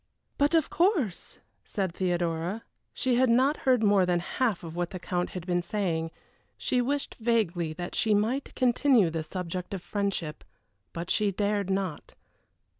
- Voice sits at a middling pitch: No, high, 195 Hz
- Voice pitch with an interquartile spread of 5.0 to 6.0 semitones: Yes, wide, 5.4 semitones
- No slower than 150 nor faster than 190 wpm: Yes, average, 155 wpm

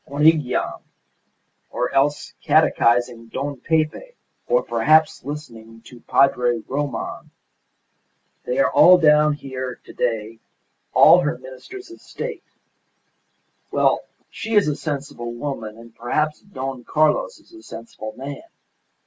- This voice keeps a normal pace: No, slow, 120 wpm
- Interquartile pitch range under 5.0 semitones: Yes, average, 4.3 semitones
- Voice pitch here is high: No, medium, 140 Hz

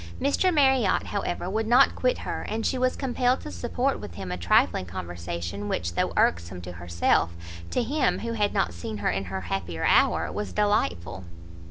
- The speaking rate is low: No, average, 185 wpm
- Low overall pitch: Yes, low, 100 Hz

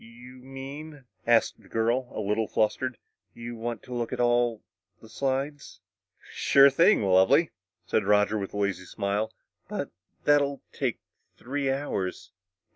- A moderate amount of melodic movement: Yes, average, 3.9 semitones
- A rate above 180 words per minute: No, average, 150 wpm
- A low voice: Yes, low, 120 Hz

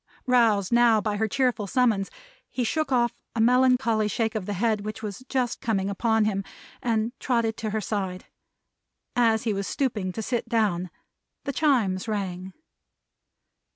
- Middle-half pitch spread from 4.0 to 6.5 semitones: No, average, 2.9 semitones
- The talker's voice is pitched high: Yes, high, 220 Hz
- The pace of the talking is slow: No, average, 155 wpm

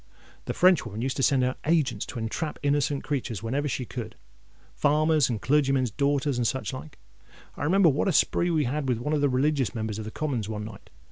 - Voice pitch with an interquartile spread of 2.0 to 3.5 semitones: No, average, 4.1 semitones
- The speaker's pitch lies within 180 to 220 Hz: No, low, 135 Hz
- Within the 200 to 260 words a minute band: Yes, fast, 205 wpm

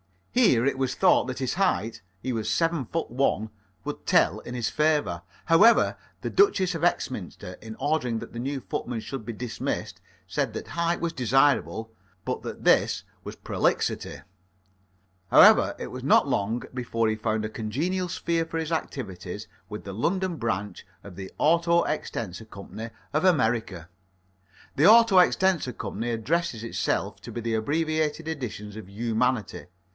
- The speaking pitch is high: No, low, 125 Hz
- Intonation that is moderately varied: No, wide, 6.7 semitones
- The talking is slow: No, average, 155 wpm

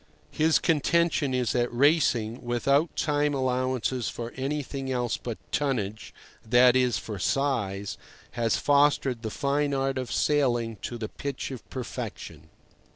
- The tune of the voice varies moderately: Yes, average, 3.2 semitones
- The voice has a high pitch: No, low, 130 Hz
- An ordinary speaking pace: No, slow, 125 wpm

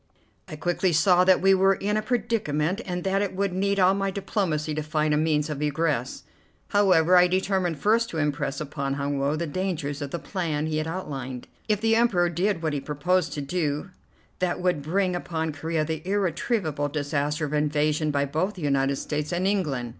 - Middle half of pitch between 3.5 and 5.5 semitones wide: Yes, average, 4.1 semitones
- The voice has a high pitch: No, medium, 160 Hz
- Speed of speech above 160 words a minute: Yes, average, 200 wpm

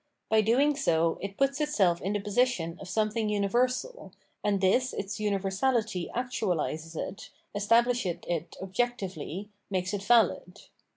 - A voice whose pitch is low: No, high, 205 Hz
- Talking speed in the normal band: No, slow, 130 wpm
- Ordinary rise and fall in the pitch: Yes, average, 4.5 semitones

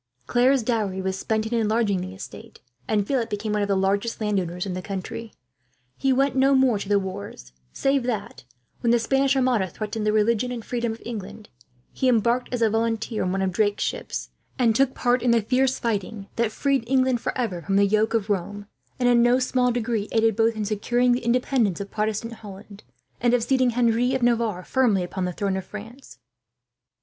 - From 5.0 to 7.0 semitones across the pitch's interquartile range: No, average, 3.3 semitones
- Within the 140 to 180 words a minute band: No, fast, 205 wpm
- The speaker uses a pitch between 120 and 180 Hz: No, high, 225 Hz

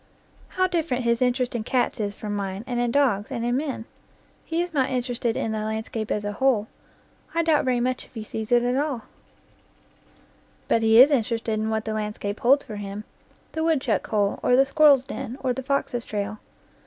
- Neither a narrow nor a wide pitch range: Yes, average, 3.6 semitones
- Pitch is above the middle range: Yes, high, 240 Hz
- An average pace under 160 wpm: No, fast, 205 wpm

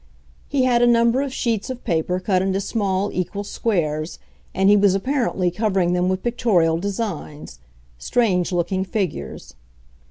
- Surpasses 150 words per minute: No, average, 145 wpm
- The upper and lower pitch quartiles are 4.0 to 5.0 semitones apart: Yes, average, 4.6 semitones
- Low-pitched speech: No, high, 190 Hz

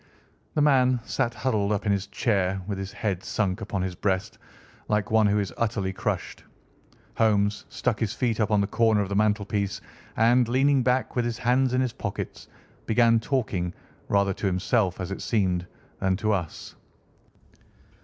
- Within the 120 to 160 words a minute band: No, average, 175 wpm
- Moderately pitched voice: No, low, 105 Hz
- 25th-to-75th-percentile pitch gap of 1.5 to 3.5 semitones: Yes, average, 3.2 semitones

